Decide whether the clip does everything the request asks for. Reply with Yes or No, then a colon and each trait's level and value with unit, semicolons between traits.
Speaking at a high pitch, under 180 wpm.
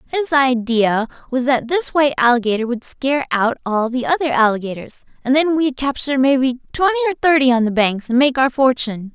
No: very high, 265 Hz; average, 190 wpm